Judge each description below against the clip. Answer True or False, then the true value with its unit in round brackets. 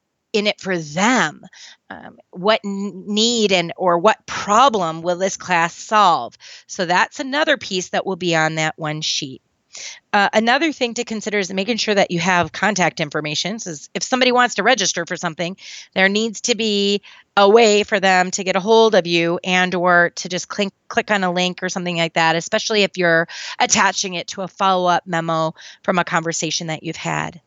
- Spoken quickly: False (195 wpm)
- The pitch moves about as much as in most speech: True (3.5 semitones)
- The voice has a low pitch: False (190 Hz)